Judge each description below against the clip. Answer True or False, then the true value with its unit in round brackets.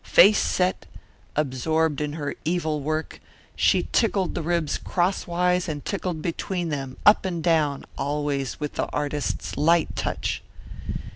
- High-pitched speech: False (160 Hz)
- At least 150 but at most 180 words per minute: False (135 wpm)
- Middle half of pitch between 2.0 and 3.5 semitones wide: True (3.2 semitones)